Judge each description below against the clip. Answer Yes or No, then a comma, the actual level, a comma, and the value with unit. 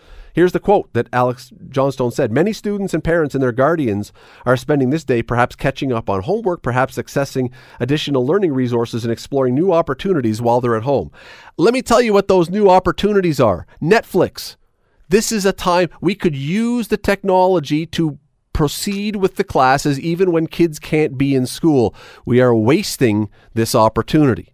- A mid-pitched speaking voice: Yes, medium, 145 Hz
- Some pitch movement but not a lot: No, wide, 6.8 semitones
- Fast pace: No, average, 175 wpm